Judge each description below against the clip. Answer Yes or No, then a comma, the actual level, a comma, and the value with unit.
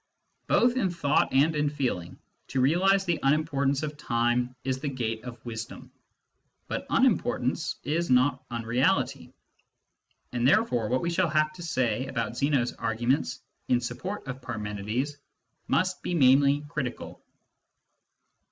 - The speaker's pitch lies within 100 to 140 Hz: Yes, low, 135 Hz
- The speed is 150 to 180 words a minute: No, slow, 135 wpm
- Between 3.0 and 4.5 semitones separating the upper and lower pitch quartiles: Yes, average, 4.1 semitones